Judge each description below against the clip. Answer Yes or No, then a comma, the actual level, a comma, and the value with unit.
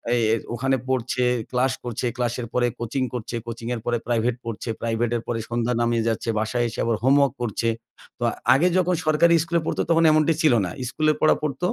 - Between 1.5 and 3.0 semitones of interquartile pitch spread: No, average, 3.5 semitones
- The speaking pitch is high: No, low, 125 Hz